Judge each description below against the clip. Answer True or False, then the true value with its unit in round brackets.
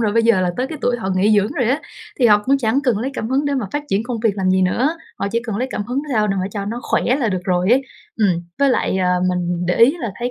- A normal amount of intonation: True (4.9 semitones)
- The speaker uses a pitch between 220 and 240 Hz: True (225 Hz)